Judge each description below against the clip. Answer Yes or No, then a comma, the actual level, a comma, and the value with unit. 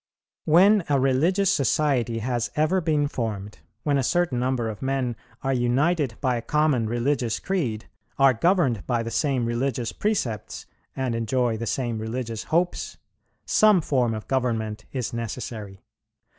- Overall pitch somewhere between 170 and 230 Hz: No, low, 125 Hz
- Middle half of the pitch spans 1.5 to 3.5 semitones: No, average, 4.4 semitones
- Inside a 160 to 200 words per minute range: No, average, 145 wpm